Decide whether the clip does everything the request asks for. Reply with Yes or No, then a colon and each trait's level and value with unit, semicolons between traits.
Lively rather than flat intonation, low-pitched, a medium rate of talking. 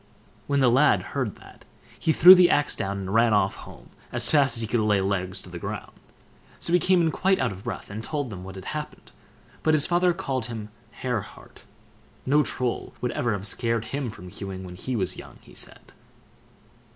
No: wide, 6.6 semitones; low, 120 Hz; fast, 210 wpm